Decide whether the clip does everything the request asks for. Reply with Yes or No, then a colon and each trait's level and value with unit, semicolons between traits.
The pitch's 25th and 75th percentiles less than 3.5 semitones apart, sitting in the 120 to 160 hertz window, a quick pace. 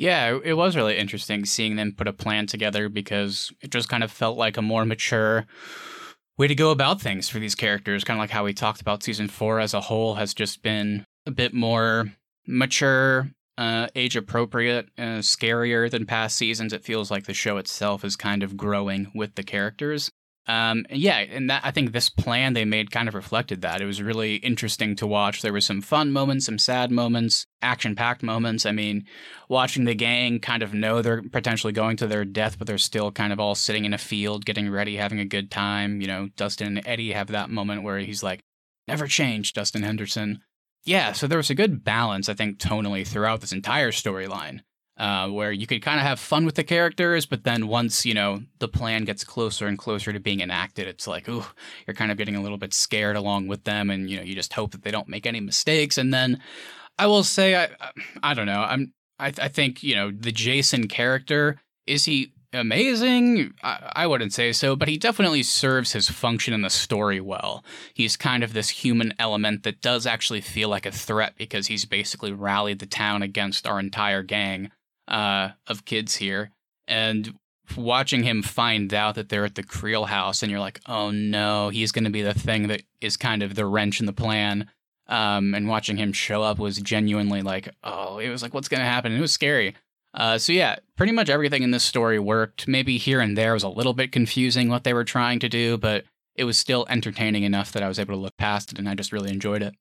No: average, 2.9 semitones; low, 110 Hz; fast, 220 wpm